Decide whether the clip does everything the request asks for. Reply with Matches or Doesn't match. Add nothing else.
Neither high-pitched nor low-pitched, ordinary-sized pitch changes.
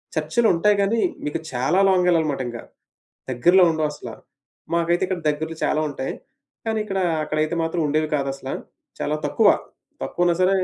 Matches